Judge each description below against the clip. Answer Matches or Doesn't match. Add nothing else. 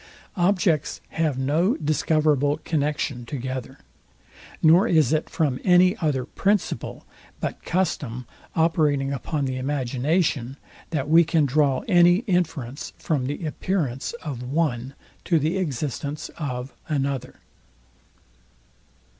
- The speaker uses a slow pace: Matches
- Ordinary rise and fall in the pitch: Matches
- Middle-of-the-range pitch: Matches